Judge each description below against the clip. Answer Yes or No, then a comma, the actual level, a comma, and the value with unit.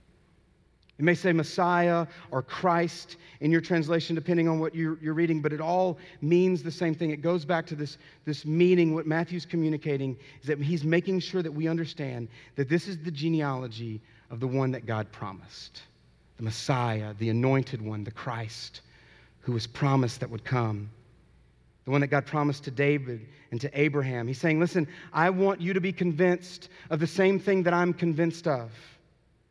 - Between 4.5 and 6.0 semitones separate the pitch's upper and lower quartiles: Yes, average, 5.0 semitones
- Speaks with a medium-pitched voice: Yes, medium, 155 Hz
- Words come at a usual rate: Yes, average, 185 wpm